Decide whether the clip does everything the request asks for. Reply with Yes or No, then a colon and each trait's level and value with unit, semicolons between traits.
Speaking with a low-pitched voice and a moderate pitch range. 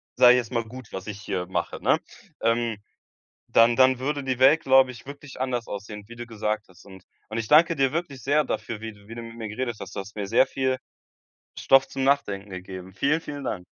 Yes: low, 120 Hz; average, 4.2 semitones